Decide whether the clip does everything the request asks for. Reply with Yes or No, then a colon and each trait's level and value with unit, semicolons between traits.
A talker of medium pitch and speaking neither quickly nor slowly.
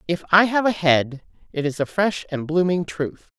No: medium, 170 Hz; fast, 215 wpm